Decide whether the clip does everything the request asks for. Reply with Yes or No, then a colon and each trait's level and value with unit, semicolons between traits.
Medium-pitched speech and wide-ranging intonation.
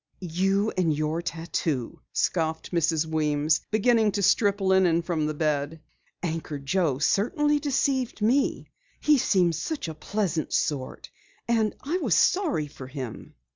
Yes: medium, 170 Hz; wide, 5.9 semitones